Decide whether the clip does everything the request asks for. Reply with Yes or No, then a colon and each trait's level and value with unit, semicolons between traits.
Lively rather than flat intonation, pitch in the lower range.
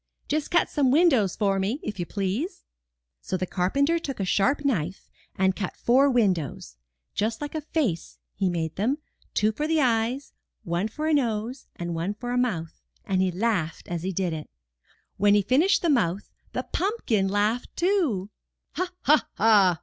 No: wide, 7.0 semitones; high, 215 Hz